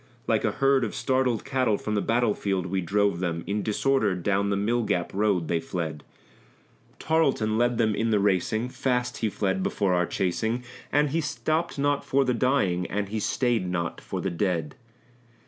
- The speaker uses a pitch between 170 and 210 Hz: No, low, 105 Hz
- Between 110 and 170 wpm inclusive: No, average, 180 wpm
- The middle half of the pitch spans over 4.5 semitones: Yes, average, 4.9 semitones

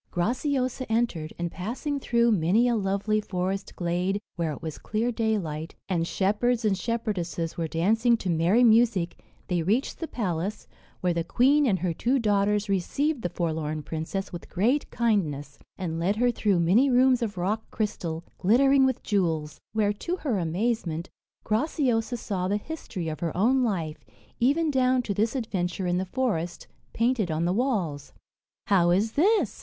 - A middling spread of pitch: No, wide, 5.7 semitones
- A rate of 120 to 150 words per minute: No, average, 165 wpm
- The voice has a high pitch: Yes, high, 205 Hz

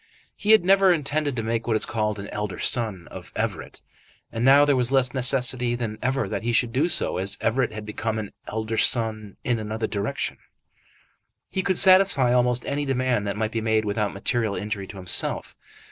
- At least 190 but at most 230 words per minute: Yes, average, 195 wpm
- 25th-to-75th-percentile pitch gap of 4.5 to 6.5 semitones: No, average, 3.7 semitones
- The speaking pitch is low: Yes, low, 115 Hz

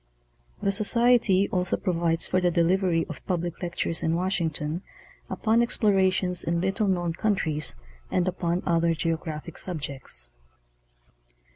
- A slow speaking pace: Yes, slow, 125 wpm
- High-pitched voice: No, medium, 175 Hz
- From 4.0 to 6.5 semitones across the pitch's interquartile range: No, narrow, 2.5 semitones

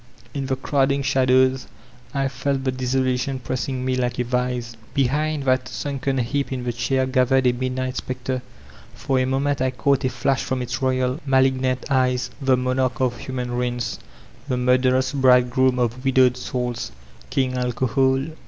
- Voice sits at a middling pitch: No, low, 130 Hz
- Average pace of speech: Yes, average, 160 wpm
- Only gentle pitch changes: Yes, narrow, 1.0 semitones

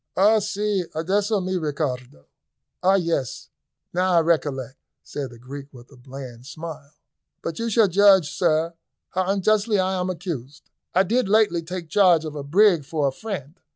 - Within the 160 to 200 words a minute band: Yes, average, 165 wpm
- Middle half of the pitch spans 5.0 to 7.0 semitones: Yes, wide, 5.4 semitones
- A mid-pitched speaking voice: Yes, medium, 170 Hz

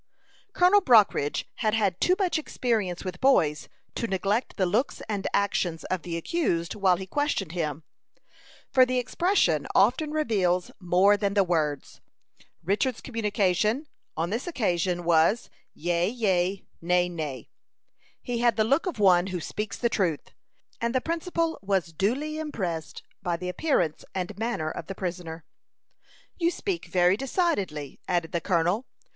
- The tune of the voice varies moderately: No, wide, 5.7 semitones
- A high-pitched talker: Yes, high, 195 Hz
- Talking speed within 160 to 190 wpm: No, average, 150 wpm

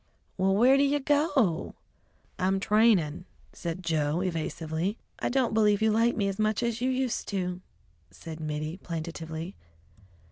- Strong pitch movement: Yes, wide, 5.7 semitones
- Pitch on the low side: No, high, 195 Hz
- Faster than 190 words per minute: No, average, 145 wpm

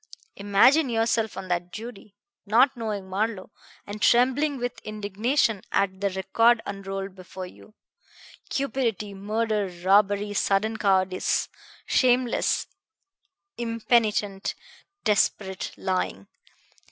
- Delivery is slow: Yes, slow, 95 wpm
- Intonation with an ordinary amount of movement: Yes, average, 3.0 semitones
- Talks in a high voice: Yes, high, 210 Hz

